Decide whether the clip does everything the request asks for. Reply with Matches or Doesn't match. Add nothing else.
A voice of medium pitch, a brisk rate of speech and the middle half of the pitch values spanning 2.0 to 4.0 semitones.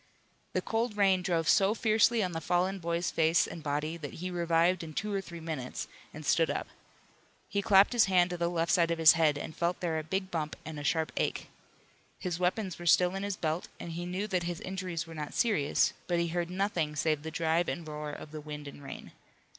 Matches